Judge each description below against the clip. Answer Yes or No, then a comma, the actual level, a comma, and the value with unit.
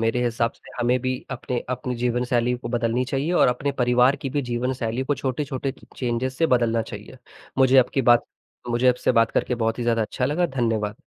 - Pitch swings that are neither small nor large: No, narrow, 1.8 semitones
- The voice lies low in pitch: Yes, low, 125 Hz